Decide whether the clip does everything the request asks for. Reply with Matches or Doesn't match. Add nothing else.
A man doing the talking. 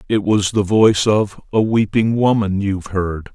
Matches